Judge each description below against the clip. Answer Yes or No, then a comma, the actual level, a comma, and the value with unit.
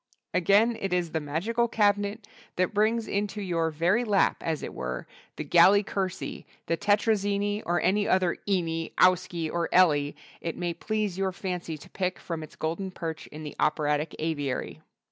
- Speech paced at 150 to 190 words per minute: Yes, average, 170 wpm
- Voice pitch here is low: No, medium, 180 Hz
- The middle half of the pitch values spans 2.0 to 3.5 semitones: No, average, 3.9 semitones